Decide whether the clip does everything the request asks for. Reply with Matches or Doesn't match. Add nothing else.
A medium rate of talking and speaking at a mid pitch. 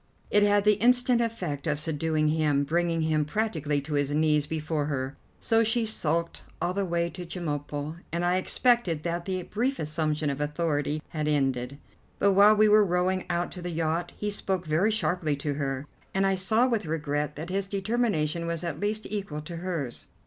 Matches